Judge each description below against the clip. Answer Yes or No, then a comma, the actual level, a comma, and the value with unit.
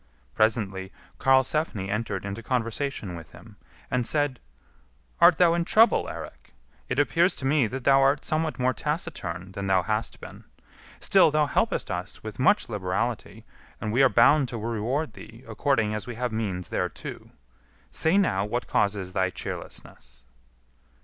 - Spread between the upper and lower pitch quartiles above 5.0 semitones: Yes, wide, 5.5 semitones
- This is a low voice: Yes, low, 120 Hz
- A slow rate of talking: No, average, 155 wpm